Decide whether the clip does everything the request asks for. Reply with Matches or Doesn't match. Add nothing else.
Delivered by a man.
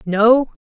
Doesn't match